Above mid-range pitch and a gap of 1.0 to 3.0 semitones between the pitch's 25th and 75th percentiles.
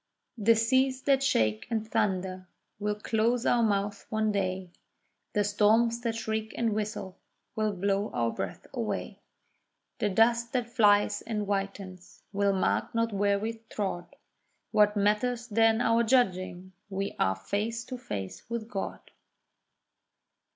Yes: high, 210 Hz; average, 2.7 semitones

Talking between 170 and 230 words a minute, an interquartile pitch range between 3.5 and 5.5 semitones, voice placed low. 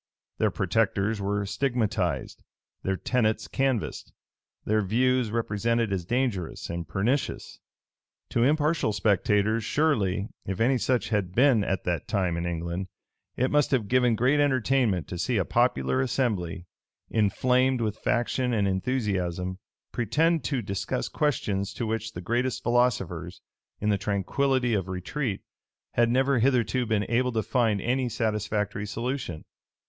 No: slow, 135 wpm; average, 4.5 semitones; low, 110 Hz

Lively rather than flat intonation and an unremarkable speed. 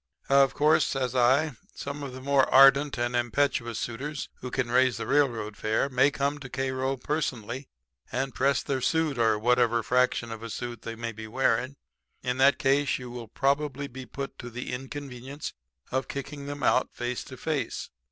No: narrow, 2.6 semitones; average, 180 wpm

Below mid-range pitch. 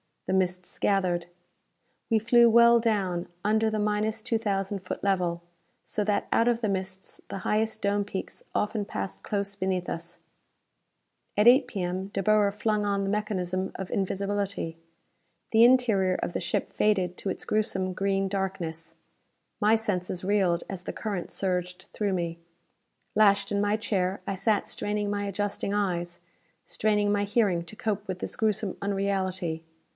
No: high, 200 Hz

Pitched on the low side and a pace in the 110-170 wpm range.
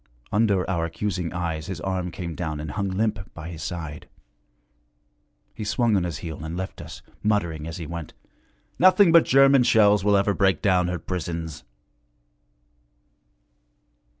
Yes: very low, 90 Hz; average, 150 wpm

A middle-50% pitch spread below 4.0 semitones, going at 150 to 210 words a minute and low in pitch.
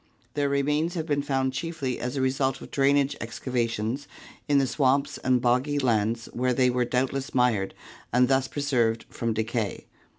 Yes: narrow, 2.6 semitones; average, 165 wpm; low, 130 Hz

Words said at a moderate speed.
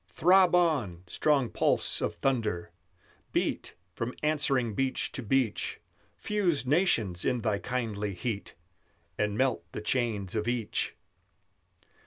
No: slow, 120 wpm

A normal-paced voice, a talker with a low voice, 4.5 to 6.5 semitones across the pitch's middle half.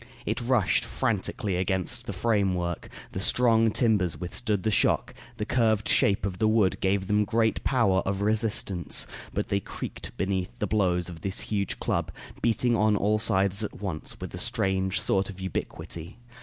No: average, 170 wpm; low, 100 Hz; narrow, 2.6 semitones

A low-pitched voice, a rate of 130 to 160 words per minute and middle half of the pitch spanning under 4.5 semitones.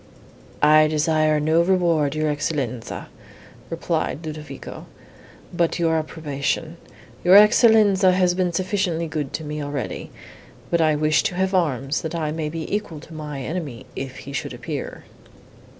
No: medium, 155 Hz; average, 145 wpm; average, 2.7 semitones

